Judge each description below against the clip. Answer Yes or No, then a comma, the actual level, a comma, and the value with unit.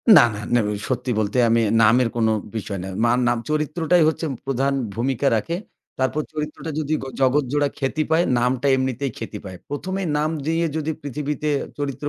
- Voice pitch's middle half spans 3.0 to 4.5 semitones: Yes, average, 4.0 semitones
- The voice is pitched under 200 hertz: Yes, medium, 140 Hz